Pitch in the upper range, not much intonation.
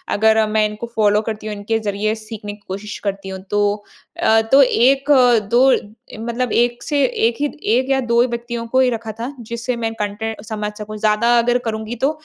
Yes: high, 225 Hz; narrow, 2.3 semitones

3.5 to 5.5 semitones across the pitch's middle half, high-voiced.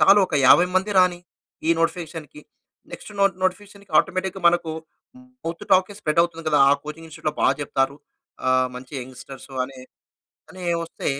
No: average, 4.3 semitones; medium, 165 Hz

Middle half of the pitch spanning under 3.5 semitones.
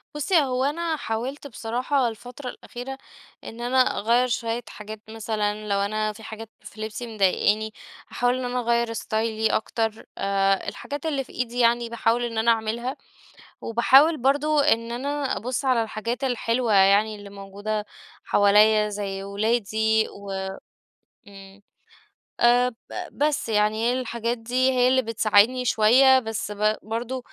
Yes: average, 2.8 semitones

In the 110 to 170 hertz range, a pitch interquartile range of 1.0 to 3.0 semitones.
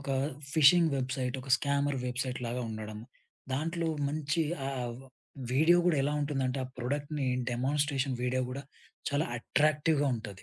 Yes: medium, 140 Hz; average, 2.7 semitones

